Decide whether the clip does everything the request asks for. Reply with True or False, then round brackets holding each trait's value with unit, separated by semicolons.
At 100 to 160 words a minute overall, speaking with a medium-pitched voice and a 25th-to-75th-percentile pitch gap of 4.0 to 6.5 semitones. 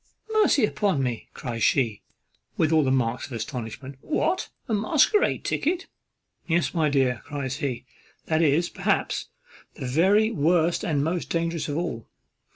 True (150 wpm; 155 Hz; 5.3 semitones)